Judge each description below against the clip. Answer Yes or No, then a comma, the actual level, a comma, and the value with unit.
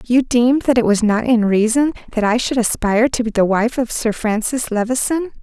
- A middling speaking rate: No, fast, 220 wpm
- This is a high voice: Yes, high, 235 Hz